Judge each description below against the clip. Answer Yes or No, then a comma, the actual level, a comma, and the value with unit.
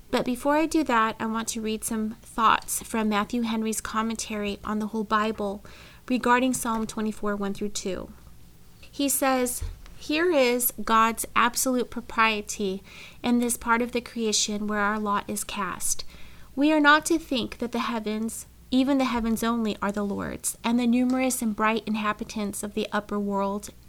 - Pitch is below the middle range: No, high, 225 Hz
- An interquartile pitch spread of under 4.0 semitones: Yes, average, 2.8 semitones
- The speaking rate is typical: Yes, average, 170 wpm